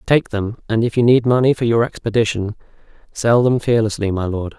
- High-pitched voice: No, low, 115 Hz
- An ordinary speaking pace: Yes, average, 195 wpm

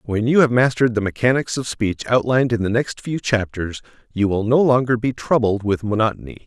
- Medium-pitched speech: No, low, 115 Hz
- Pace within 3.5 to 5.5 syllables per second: No, 5.7 syllables/s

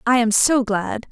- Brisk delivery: Yes, fast, 215 wpm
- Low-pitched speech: No, high, 230 Hz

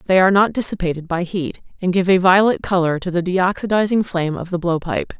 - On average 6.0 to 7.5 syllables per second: Yes, 6.2 syllables/s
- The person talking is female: Yes, female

